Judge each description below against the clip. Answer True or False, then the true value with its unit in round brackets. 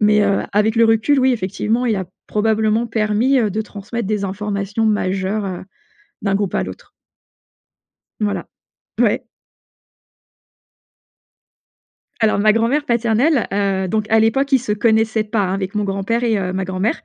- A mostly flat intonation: True (2.3 semitones)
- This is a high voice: True (215 Hz)